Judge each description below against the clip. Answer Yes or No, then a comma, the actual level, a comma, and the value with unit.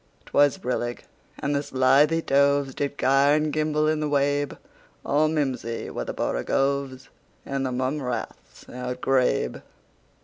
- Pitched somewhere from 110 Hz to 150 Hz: Yes, medium, 140 Hz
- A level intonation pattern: Yes, narrow, 2.1 semitones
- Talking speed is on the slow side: Yes, slow, 125 wpm